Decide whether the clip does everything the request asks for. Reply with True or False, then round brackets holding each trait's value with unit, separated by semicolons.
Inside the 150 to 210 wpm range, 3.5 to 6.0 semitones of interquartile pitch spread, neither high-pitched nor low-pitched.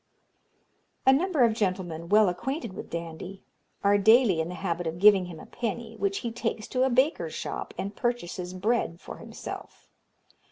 False (170 wpm; 5.0 semitones; 205 Hz)